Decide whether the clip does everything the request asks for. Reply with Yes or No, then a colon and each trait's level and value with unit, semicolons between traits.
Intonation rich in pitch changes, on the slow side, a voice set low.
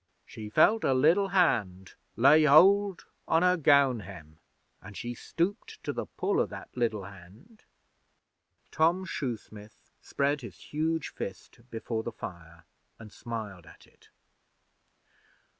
Yes: wide, 8.4 semitones; slow, 130 wpm; low, 125 Hz